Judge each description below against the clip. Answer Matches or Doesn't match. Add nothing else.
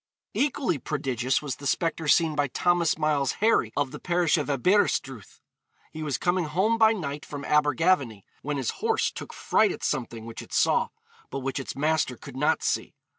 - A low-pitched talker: Doesn't match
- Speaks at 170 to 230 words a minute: Matches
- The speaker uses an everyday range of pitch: Matches